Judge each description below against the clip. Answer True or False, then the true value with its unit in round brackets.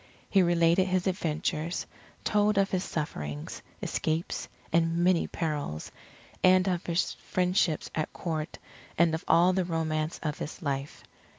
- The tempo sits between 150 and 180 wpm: False (140 wpm)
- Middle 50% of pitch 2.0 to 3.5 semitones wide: True (2.8 semitones)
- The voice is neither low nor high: True (170 Hz)